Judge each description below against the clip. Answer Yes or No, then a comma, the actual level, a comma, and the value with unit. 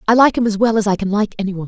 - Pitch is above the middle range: Yes, high, 210 Hz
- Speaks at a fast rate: Yes, fast, 395 wpm